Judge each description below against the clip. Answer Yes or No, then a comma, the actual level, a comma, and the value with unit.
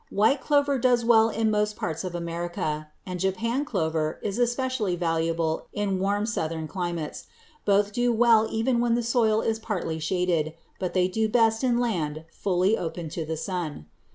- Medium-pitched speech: No, high, 195 Hz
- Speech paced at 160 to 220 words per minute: Yes, average, 175 wpm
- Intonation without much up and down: No, wide, 5.4 semitones